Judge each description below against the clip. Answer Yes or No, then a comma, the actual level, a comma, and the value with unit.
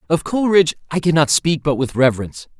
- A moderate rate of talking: No, fast, 210 wpm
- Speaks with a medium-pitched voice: Yes, medium, 150 Hz